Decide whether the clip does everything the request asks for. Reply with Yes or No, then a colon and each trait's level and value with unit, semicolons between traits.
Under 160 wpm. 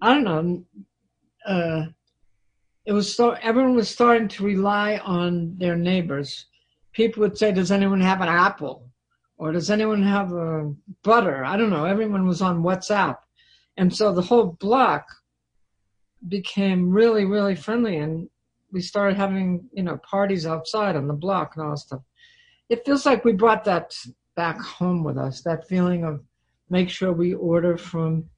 No: average, 165 wpm